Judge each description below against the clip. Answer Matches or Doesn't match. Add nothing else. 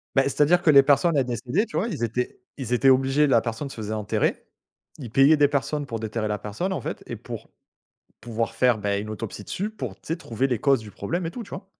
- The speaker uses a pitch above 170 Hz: Doesn't match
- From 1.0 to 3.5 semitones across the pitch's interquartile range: Doesn't match